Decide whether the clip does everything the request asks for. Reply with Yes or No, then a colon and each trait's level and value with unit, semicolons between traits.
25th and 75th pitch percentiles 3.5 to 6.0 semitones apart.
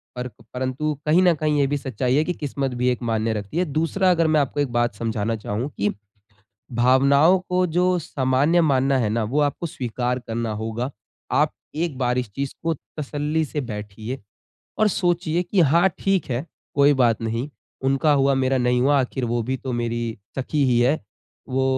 Yes: average, 4.1 semitones